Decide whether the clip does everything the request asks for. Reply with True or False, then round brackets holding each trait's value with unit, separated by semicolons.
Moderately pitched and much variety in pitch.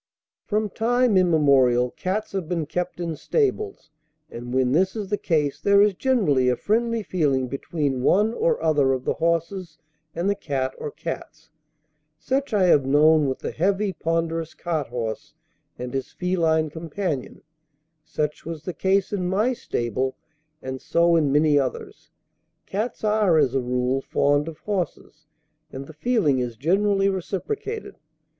True (165 Hz; 6.1 semitones)